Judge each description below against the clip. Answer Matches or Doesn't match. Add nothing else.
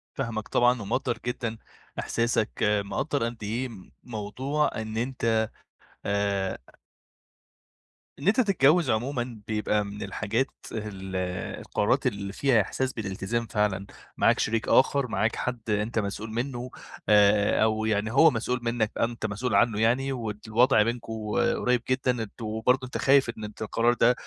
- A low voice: Matches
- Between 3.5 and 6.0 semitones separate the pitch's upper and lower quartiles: Doesn't match